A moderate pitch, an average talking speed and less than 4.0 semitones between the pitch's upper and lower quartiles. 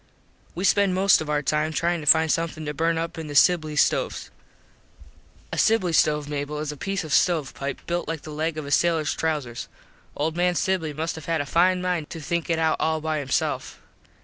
No: medium, 160 Hz; fast, 215 wpm; narrow, 2.4 semitones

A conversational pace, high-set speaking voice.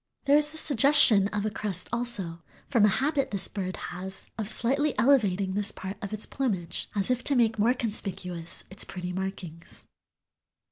Yes: average, 175 wpm; high, 210 Hz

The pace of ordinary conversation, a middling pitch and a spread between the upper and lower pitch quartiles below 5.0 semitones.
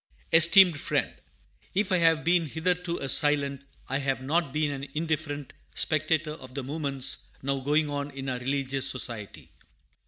Yes: average, 155 wpm; medium, 145 Hz; average, 2.9 semitones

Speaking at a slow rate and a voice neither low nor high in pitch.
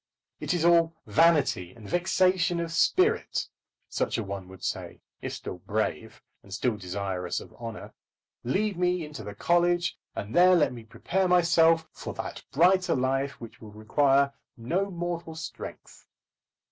No: average, 150 wpm; medium, 160 Hz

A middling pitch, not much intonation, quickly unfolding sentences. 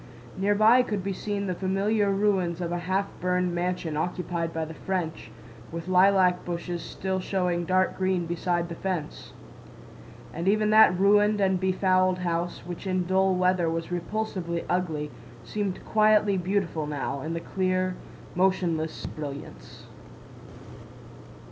No: medium, 180 Hz; narrow, 2.1 semitones; slow, 135 wpm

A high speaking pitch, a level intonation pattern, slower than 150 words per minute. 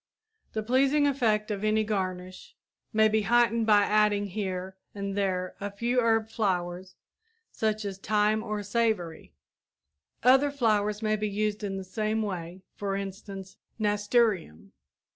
Yes: high, 210 Hz; narrow, 2.1 semitones; average, 140 wpm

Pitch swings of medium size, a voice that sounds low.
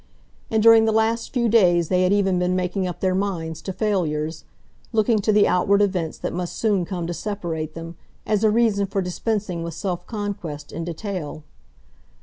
No: average, 3.6 semitones; high, 190 Hz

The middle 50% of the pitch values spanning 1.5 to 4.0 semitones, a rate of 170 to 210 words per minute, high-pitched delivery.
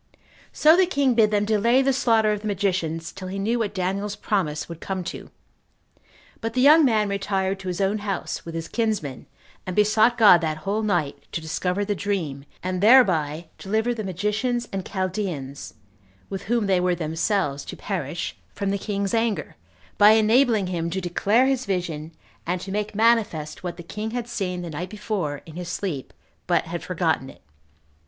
Yes: average, 3.7 semitones; average, 185 wpm; high, 195 Hz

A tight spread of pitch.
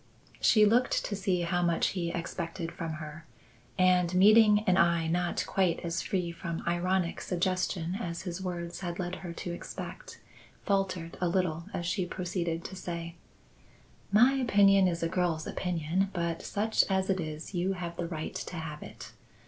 Yes: narrow, 2.0 semitones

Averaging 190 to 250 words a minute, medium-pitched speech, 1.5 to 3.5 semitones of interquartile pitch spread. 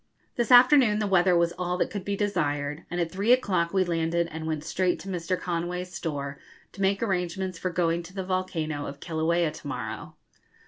Yes: average, 195 wpm; medium, 175 Hz; narrow, 2.6 semitones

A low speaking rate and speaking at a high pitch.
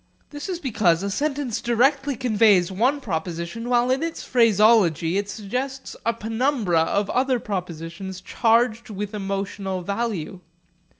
Yes: slow, 130 wpm; high, 220 Hz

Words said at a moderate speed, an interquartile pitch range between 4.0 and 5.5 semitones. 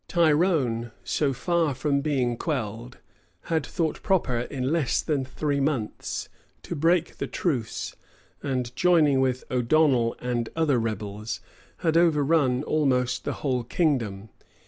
No: slow, 125 wpm; average, 4.3 semitones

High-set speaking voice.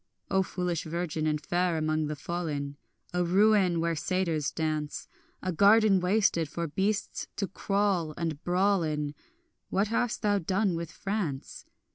No: medium, 175 Hz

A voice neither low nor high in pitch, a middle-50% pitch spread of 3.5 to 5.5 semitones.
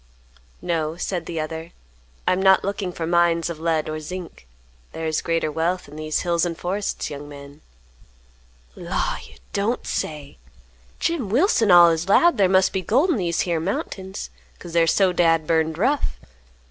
No: medium, 170 Hz; average, 3.0 semitones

